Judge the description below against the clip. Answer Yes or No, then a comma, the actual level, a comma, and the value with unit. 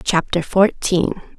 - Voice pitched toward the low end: No, medium, 180 Hz